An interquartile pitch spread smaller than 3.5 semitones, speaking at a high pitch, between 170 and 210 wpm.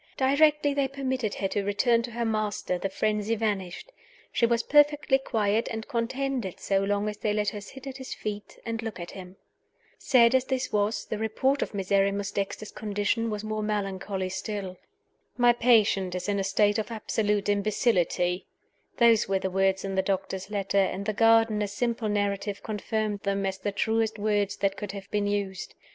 Yes: narrow, 2.6 semitones; high, 210 Hz; average, 185 wpm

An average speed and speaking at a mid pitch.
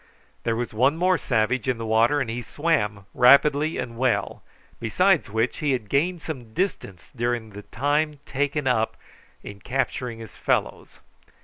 No: average, 155 wpm; low, 125 Hz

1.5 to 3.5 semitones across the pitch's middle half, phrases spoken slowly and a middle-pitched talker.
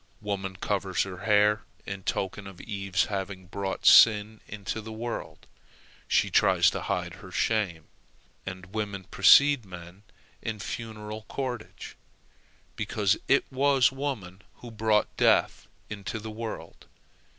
No: narrow, 2.5 semitones; slow, 130 wpm; low, 105 Hz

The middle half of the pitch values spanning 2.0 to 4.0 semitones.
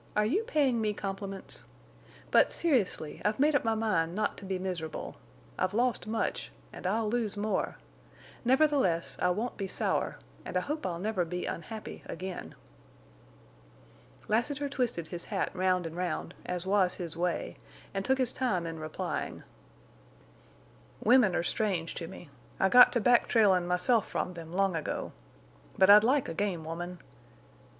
No: average, 4.4 semitones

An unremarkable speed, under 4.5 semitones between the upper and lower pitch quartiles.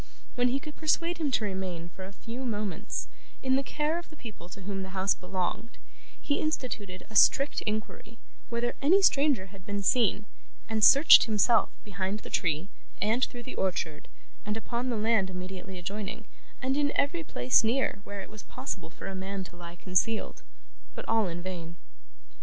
No: average, 180 wpm; average, 5.3 semitones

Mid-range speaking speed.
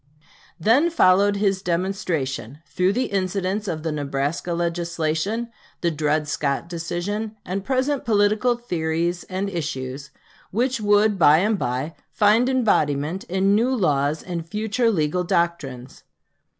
No: slow, 125 wpm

